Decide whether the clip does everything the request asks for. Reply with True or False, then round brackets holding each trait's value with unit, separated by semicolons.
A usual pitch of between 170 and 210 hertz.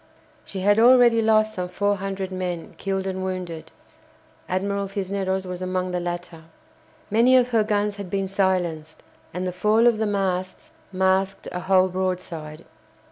True (190 Hz)